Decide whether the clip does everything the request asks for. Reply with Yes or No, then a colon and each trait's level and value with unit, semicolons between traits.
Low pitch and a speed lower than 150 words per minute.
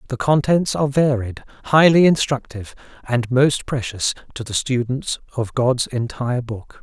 Yes: low, 130 Hz; average, 140 wpm